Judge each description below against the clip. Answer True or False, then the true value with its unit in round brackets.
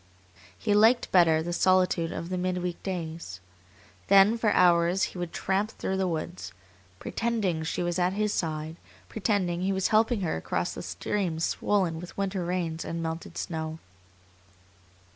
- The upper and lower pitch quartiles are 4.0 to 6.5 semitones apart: False (2.8 semitones)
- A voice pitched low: False (180 Hz)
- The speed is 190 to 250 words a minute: False (155 wpm)